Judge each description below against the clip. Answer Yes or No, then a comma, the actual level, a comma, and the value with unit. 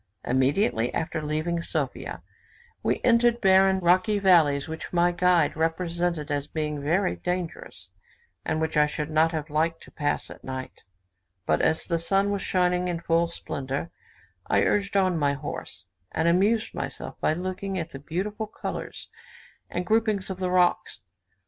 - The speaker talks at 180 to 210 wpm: No, average, 155 wpm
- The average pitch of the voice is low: No, medium, 170 Hz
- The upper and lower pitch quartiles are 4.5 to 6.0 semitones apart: No, average, 3.4 semitones